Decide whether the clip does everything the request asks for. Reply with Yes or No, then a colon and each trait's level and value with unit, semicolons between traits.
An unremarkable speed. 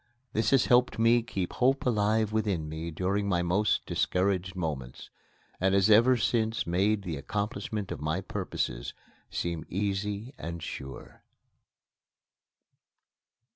No: slow, 125 wpm